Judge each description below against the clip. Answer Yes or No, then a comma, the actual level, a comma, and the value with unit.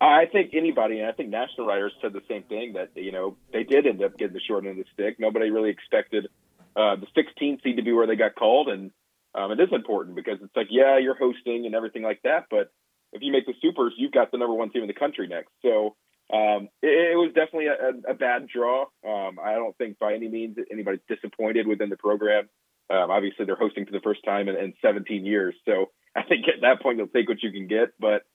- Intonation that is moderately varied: No, wide, 8.2 semitones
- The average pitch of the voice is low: Yes, low, 120 Hz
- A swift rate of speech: Yes, fast, 250 wpm